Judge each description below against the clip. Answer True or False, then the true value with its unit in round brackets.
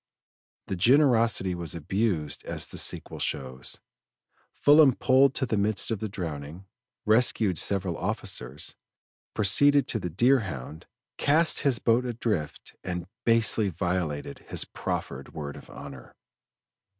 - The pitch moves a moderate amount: False (6.8 semitones)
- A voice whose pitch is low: True (100 Hz)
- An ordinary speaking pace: False (125 wpm)